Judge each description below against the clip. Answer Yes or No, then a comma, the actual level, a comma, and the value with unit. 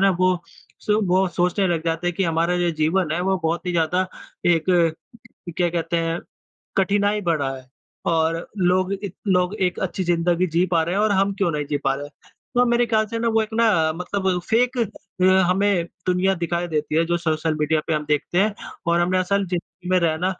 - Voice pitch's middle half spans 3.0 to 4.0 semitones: No, narrow, 2.6 semitones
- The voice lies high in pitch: No, medium, 180 Hz